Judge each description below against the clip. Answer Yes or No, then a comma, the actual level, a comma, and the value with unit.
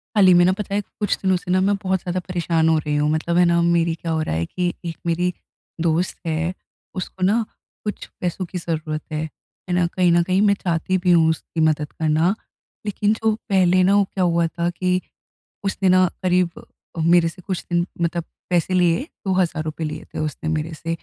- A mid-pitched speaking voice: Yes, medium, 175 Hz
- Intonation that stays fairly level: Yes, narrow, 2.2 semitones